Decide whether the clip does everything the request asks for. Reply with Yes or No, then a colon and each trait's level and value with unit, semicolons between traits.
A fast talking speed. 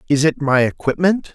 No: average, 180 wpm